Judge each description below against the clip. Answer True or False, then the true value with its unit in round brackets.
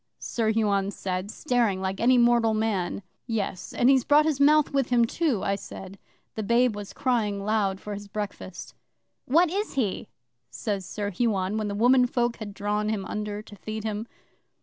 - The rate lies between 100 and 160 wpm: False (175 wpm)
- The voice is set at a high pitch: True (215 Hz)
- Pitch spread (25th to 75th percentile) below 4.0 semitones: True (3.3 semitones)